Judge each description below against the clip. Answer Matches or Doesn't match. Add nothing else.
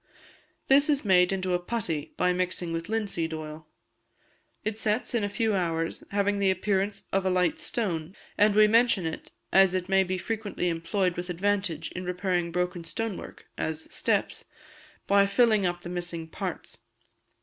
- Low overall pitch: Doesn't match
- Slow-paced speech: Doesn't match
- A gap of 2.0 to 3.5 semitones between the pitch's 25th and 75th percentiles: Matches